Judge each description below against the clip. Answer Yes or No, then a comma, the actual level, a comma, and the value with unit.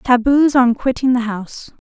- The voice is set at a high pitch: Yes, very high, 250 Hz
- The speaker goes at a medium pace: Yes, average, 160 wpm